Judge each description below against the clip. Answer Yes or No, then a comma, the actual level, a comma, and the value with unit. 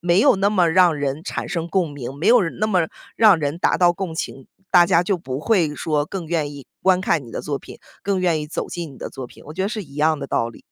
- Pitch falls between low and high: Yes, medium, 170 Hz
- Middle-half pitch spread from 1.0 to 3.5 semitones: No, average, 4.2 semitones